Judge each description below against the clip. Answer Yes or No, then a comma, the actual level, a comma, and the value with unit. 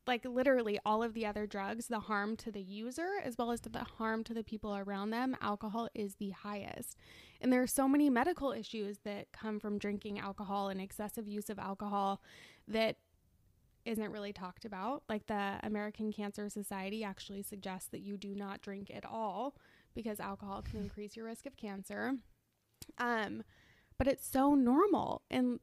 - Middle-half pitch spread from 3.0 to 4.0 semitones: No, narrow, 2.6 semitones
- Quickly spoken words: No, average, 180 wpm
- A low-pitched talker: No, high, 210 Hz